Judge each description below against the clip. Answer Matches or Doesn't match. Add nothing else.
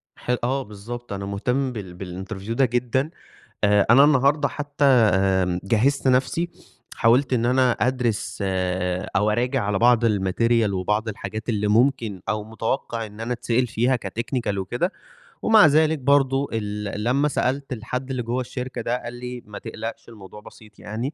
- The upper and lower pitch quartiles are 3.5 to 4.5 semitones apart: Matches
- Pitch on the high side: Doesn't match